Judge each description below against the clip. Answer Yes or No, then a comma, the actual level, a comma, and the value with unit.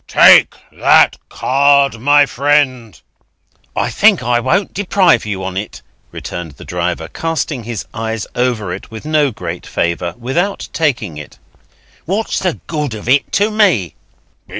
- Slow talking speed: No, average, 145 wpm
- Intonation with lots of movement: Yes, wide, 6.8 semitones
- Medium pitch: No, low, 125 Hz